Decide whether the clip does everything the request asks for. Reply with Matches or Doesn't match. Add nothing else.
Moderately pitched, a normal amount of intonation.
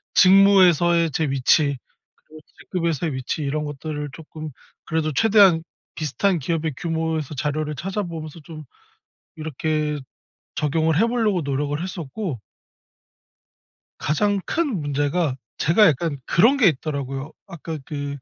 Matches